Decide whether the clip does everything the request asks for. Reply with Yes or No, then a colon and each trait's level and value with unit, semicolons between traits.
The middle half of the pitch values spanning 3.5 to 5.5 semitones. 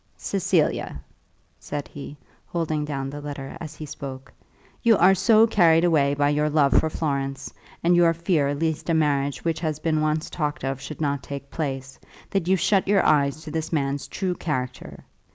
No: average, 3.0 semitones